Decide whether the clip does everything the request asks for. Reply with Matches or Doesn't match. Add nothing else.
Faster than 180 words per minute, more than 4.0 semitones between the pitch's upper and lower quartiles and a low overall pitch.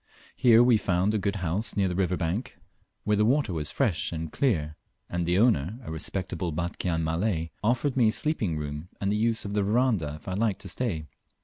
Matches